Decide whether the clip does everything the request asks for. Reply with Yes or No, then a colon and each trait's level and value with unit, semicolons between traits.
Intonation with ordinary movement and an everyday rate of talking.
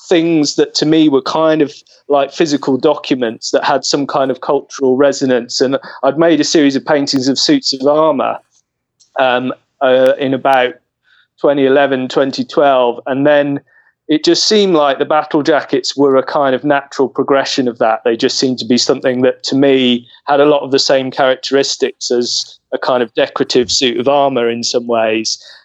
No: narrow, 2.2 semitones; average, 180 wpm